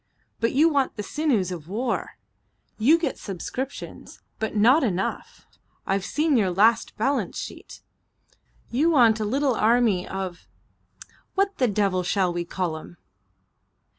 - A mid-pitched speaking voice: No, high, 220 Hz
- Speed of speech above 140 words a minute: No, slow, 135 wpm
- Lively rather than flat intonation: Yes, wide, 6.0 semitones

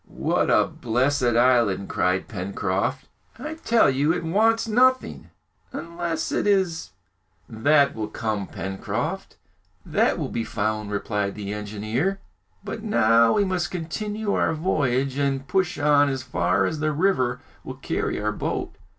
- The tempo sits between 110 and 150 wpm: Yes, average, 145 wpm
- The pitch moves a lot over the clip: Yes, wide, 8.5 semitones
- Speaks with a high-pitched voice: No, low, 135 Hz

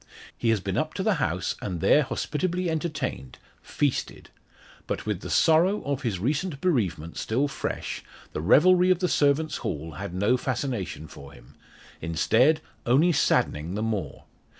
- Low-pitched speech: Yes, low, 130 Hz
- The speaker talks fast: No, average, 155 wpm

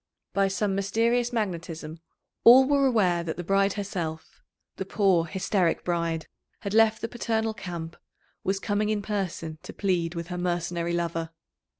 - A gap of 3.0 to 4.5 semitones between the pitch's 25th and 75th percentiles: Yes, average, 3.9 semitones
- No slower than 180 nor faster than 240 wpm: No, average, 155 wpm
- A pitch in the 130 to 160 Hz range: No, high, 190 Hz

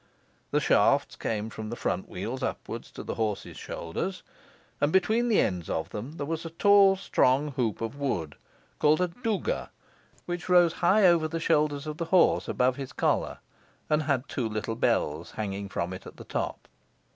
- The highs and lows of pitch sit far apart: Yes, wide, 8.0 semitones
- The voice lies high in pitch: No, medium, 145 Hz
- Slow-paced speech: No, average, 180 wpm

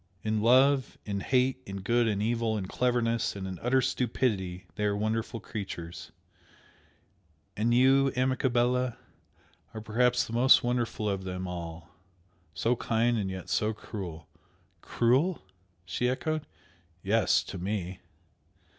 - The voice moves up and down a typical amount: Yes, average, 4.1 semitones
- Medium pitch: No, low, 115 Hz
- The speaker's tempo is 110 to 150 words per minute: Yes, slow, 135 wpm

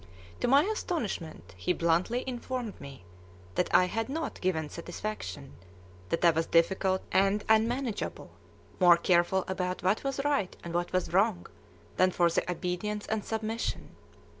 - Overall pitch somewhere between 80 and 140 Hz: No, high, 190 Hz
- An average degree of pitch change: Yes, average, 4.5 semitones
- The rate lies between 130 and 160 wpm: Yes, average, 145 wpm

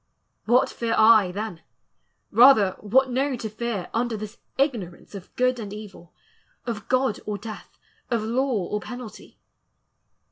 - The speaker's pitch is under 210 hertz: No, high, 225 Hz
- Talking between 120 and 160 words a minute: Yes, average, 140 wpm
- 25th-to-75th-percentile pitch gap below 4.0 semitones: Yes, average, 3.2 semitones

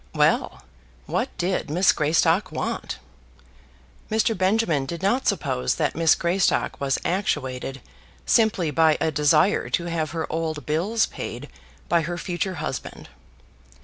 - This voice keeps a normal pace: No, slow, 130 wpm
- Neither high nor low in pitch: Yes, medium, 170 Hz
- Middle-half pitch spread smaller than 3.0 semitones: No, average, 3.8 semitones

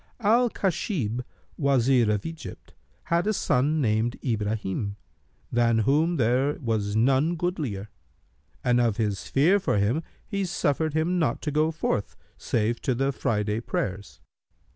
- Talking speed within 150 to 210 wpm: No, average, 140 wpm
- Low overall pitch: Yes, low, 130 Hz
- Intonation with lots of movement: Yes, wide, 6.4 semitones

